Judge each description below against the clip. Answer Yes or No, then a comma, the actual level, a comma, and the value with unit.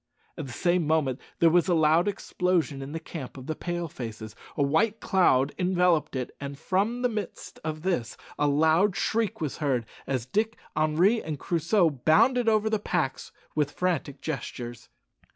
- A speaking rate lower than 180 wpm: Yes, average, 170 wpm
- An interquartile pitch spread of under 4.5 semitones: No, average, 4.8 semitones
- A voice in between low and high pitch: Yes, medium, 160 Hz